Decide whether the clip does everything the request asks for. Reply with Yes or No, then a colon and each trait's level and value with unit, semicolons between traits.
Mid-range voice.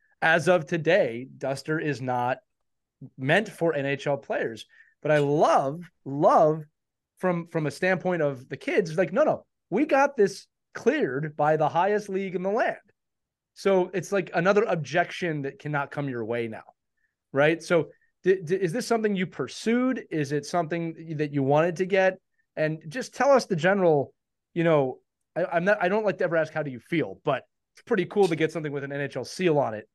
Yes: medium, 165 Hz